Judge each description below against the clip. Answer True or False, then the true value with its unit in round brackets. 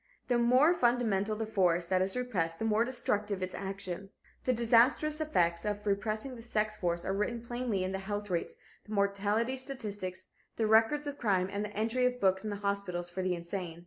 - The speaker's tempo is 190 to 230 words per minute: True (195 wpm)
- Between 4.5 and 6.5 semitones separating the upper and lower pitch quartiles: False (3.9 semitones)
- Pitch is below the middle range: False (210 Hz)